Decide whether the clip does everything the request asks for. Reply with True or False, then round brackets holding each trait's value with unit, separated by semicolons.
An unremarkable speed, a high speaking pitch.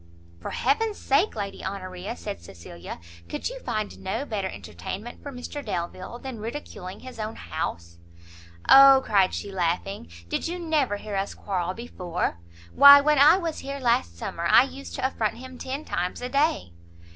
True (170 wpm; 215 Hz)